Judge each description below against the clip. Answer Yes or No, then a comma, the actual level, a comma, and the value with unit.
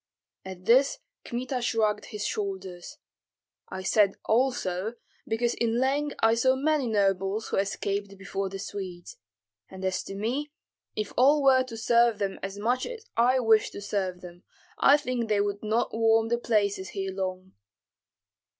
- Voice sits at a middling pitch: No, high, 215 Hz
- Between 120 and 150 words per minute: No, average, 160 wpm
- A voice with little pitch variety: No, average, 3.8 semitones